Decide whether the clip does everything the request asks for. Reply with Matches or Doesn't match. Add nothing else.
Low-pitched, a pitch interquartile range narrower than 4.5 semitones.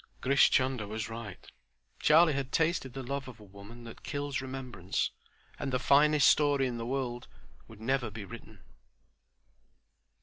Matches